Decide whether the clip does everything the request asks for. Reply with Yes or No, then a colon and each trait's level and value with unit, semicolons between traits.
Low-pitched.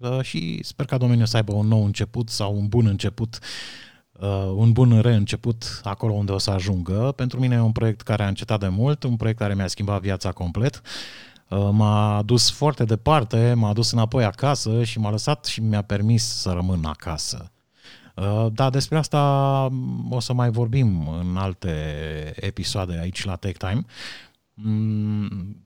Yes: low, 110 Hz